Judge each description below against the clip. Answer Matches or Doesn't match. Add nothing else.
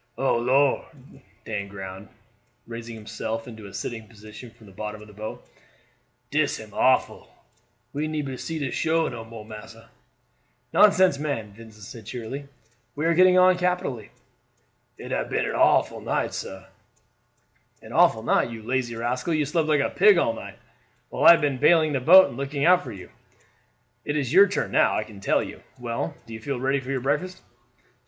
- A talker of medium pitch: Doesn't match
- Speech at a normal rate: Matches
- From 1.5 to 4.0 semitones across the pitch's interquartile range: Doesn't match